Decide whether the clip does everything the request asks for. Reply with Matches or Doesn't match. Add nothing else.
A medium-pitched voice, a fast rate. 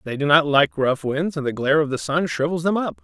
Matches